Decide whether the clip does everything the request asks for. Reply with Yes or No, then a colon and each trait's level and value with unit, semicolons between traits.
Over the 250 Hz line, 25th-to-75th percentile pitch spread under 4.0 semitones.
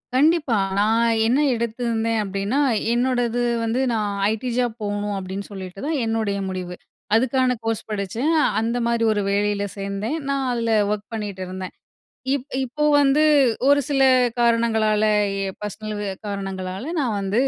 No: high, 225 Hz; average, 3.3 semitones